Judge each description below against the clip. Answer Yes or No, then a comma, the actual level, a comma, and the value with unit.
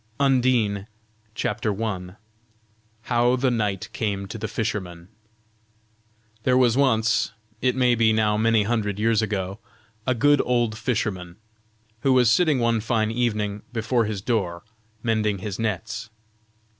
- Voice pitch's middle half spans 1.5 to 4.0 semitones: Yes, average, 2.7 semitones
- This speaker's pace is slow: Yes, slow, 130 wpm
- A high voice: No, low, 110 Hz